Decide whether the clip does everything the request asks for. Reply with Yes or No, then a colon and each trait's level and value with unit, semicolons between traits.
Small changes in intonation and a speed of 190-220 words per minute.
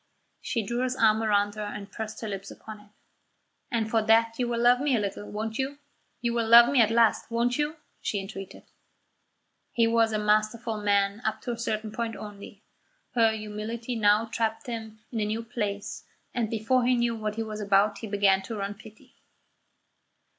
Yes: narrow, 1.9 semitones; average, 195 wpm